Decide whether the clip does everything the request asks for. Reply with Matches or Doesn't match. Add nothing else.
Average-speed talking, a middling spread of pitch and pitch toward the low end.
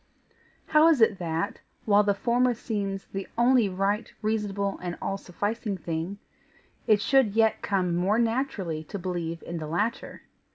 Doesn't match